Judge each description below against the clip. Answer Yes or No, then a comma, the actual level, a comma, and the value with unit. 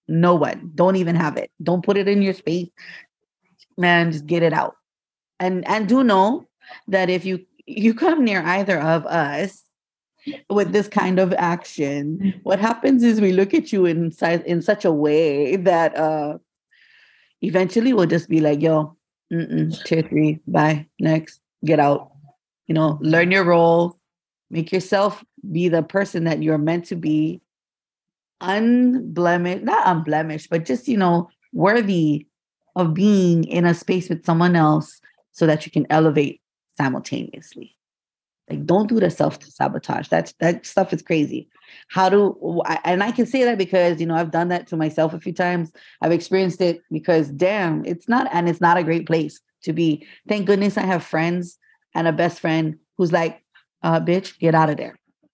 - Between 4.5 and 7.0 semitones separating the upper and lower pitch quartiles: No, average, 3.3 semitones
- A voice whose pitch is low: No, medium, 175 Hz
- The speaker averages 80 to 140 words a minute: No, average, 175 wpm